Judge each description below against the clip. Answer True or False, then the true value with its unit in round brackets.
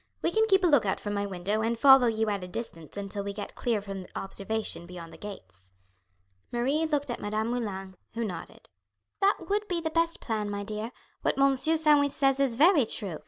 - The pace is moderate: False (210 wpm)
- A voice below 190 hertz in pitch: False (225 Hz)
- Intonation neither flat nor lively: False (6.1 semitones)